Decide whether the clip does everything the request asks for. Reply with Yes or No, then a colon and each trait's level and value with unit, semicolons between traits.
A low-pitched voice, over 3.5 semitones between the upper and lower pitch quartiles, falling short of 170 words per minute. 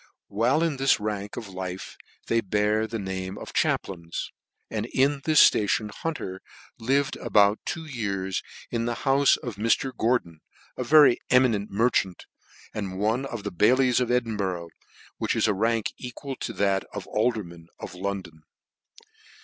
Yes: low, 110 Hz; average, 4.4 semitones; average, 155 wpm